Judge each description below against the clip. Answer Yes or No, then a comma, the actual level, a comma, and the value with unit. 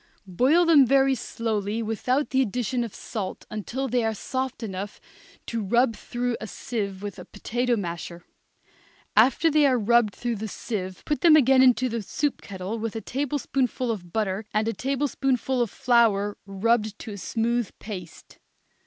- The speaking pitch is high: Yes, high, 230 Hz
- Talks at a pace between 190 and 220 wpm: No, average, 165 wpm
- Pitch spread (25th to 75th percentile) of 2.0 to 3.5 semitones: No, average, 3.9 semitones